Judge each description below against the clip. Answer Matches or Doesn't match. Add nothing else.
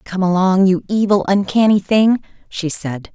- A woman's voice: Matches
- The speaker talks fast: Doesn't match